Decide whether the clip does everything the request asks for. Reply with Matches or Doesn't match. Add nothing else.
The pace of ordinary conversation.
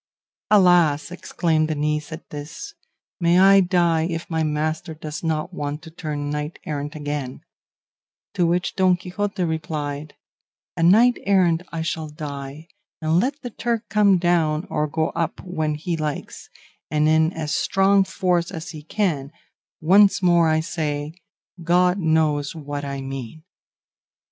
Matches